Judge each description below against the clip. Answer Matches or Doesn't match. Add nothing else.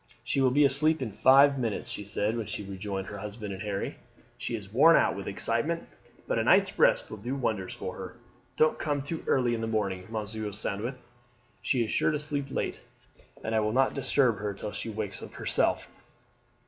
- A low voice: Matches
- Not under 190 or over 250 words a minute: Matches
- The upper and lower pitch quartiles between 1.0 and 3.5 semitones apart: Doesn't match